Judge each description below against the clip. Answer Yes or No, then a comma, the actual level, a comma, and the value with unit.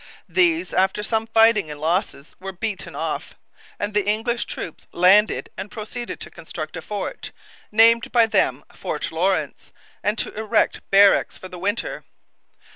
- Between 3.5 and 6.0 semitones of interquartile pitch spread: No, average, 2.8 semitones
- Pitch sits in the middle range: No, high, 210 Hz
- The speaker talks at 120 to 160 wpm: Yes, average, 150 wpm